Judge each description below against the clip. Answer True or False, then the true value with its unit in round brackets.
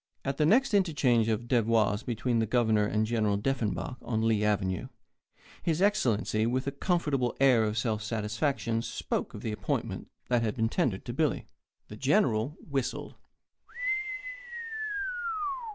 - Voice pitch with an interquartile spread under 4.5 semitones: True (4.0 semitones)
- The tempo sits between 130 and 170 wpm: True (140 wpm)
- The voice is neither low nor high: False (115 Hz)